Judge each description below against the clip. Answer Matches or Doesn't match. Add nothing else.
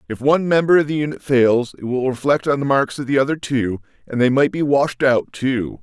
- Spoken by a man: Matches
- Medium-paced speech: Doesn't match